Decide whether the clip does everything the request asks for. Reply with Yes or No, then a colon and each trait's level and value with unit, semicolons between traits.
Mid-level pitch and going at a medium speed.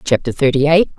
Yes: medium, 145 Hz; average, 185 wpm